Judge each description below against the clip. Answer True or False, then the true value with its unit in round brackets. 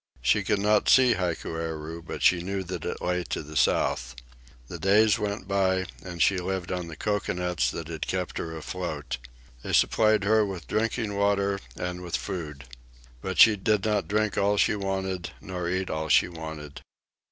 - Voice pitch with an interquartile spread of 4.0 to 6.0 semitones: False (3.3 semitones)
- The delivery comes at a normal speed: True (175 wpm)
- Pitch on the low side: True (95 Hz)